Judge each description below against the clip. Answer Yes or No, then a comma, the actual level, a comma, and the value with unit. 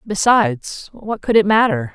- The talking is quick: No, average, 155 wpm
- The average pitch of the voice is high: Yes, high, 230 Hz